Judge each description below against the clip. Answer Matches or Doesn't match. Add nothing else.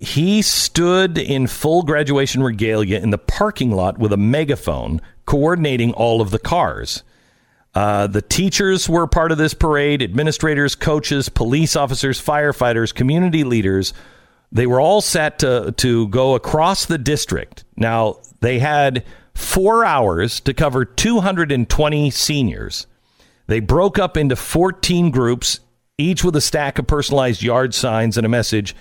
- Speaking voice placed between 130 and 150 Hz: Matches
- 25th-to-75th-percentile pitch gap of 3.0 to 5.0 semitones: Doesn't match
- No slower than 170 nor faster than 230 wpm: Doesn't match